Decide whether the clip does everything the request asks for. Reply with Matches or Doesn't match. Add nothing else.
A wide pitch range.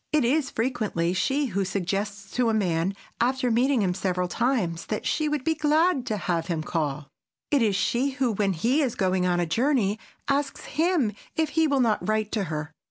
Matches